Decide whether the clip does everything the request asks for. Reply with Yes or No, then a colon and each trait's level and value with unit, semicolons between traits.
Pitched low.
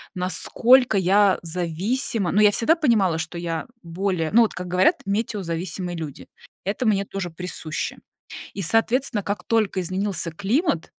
No: high, 190 Hz